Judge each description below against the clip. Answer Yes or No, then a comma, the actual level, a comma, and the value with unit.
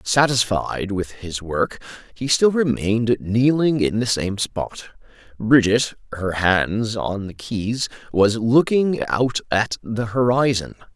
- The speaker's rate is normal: No, slow, 130 wpm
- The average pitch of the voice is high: No, low, 115 Hz